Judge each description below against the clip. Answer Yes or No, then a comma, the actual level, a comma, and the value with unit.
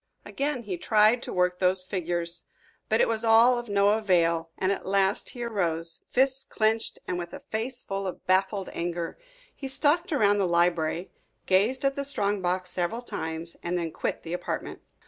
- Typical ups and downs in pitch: Yes, average, 4.6 semitones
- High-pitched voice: Yes, high, 195 Hz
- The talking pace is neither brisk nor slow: Yes, average, 185 wpm